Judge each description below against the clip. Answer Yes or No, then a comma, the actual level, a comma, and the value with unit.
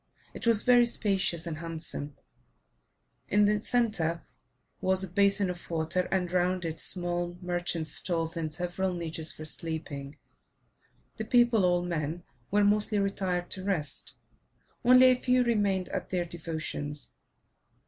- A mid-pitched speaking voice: Yes, medium, 180 Hz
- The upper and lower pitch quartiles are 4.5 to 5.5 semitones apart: No, average, 3.6 semitones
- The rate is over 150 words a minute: No, average, 140 wpm